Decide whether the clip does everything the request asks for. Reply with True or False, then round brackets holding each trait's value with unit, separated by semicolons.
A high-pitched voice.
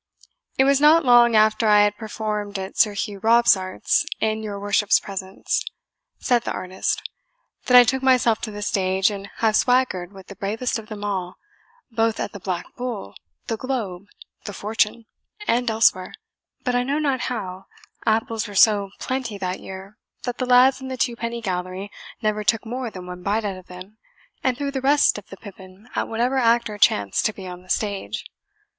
True (215 Hz)